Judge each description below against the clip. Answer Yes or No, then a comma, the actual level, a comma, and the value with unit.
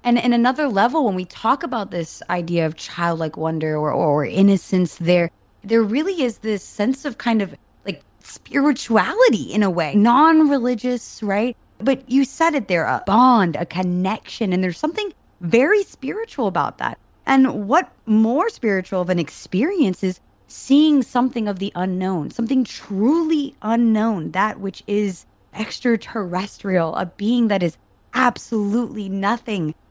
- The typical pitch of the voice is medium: No, high, 215 Hz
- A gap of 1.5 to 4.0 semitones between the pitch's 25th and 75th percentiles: No, wide, 5.6 semitones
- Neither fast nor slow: Yes, average, 150 wpm